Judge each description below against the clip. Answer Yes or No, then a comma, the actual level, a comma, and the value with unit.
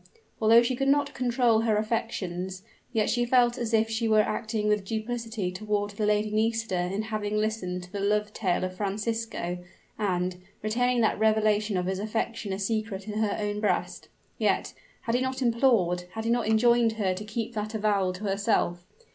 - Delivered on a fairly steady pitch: Yes, narrow, 2.3 semitones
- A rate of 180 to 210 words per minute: Yes, average, 185 wpm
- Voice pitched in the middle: No, high, 215 Hz